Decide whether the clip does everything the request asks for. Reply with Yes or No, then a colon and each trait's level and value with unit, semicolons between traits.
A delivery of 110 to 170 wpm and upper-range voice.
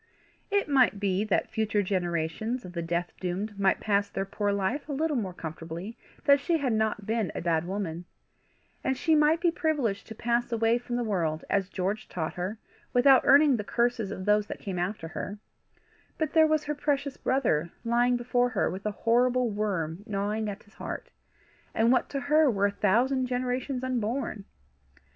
No: average, 185 wpm; high, 220 Hz